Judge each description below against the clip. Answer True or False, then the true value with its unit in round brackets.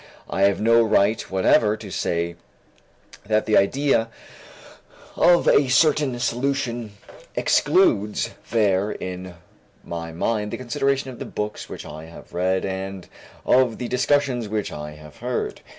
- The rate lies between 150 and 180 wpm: False (135 wpm)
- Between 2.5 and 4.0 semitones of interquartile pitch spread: False (4.9 semitones)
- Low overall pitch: True (110 Hz)